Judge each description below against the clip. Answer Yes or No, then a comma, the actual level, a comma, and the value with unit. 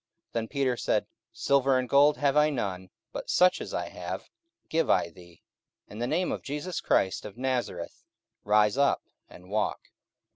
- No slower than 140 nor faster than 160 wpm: No, average, 175 wpm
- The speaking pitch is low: Yes, low, 125 Hz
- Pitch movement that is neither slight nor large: No, wide, 5.7 semitones